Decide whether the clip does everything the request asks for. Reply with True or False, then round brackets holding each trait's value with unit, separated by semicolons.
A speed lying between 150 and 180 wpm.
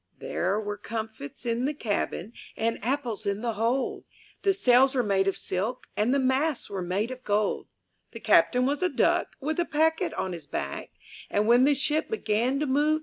False (200 wpm)